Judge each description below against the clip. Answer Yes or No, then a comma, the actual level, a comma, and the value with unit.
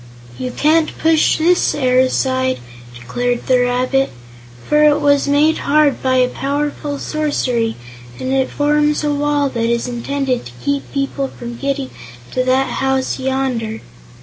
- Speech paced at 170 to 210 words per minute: No, average, 145 wpm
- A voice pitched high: Yes, very high, 270 Hz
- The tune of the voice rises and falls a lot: No, narrow, 2.5 semitones